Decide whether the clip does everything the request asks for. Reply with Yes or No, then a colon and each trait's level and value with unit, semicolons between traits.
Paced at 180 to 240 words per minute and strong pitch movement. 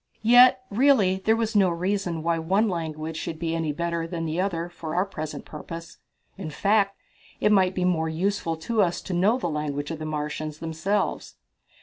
No: average, 190 wpm; average, 3.7 semitones